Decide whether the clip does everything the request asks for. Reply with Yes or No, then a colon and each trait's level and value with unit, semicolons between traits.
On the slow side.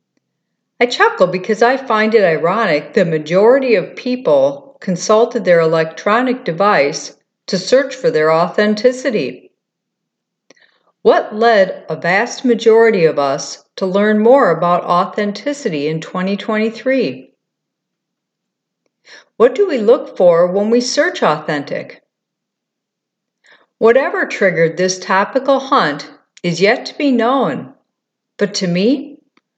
Yes: slow, 115 wpm